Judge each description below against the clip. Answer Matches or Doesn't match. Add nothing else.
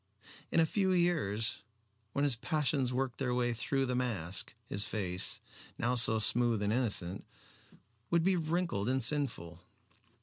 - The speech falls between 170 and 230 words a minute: Doesn't match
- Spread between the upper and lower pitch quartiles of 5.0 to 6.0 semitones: Matches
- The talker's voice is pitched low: Matches